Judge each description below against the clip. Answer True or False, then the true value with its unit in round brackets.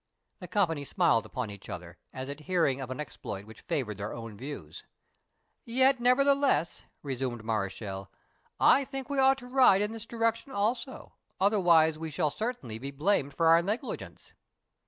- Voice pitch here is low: False (160 Hz)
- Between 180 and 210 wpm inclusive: False (160 wpm)